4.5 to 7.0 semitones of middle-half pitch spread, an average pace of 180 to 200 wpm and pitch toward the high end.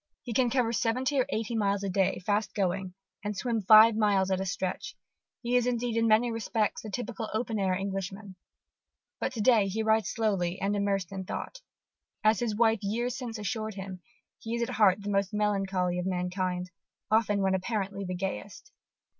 No: average, 3.0 semitones; average, 190 wpm; high, 210 Hz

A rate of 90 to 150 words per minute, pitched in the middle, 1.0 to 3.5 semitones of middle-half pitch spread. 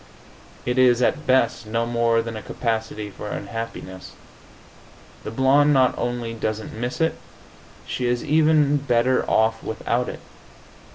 No: slow, 135 wpm; low, 120 Hz; narrow, 2.5 semitones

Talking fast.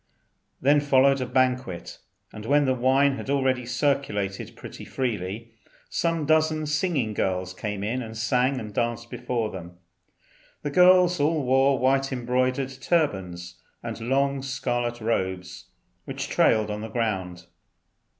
No: slow, 135 wpm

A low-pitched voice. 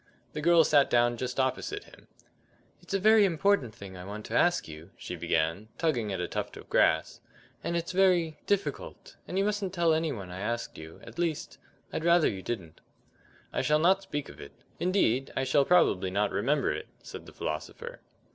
No: medium, 145 Hz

